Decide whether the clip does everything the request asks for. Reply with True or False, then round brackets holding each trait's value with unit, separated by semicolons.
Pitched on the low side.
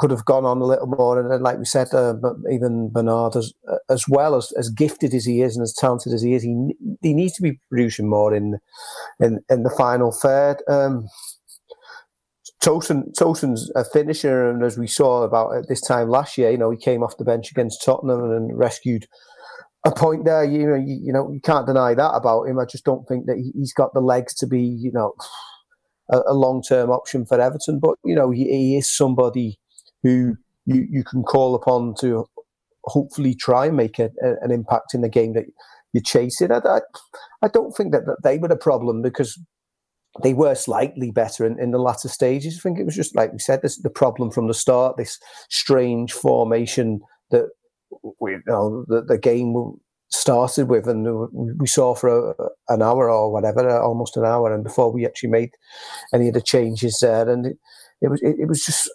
True (125 Hz)